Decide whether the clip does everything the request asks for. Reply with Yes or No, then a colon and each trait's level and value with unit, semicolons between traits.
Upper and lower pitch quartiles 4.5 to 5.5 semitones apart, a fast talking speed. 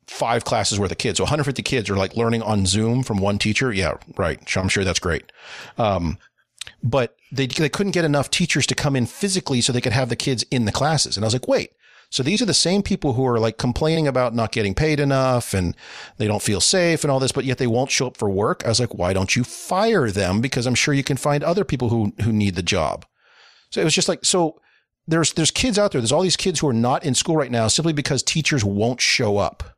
Yes: average, 5.2 semitones; fast, 260 wpm